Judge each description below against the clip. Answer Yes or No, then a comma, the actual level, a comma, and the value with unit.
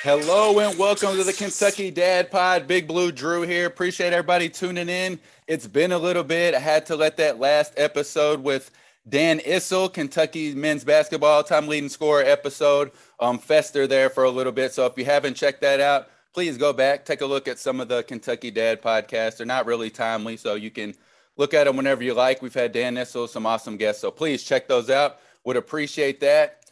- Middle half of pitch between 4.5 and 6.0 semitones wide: Yes, average, 5.1 semitones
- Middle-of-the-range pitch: Yes, medium, 150 Hz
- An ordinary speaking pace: No, fast, 210 wpm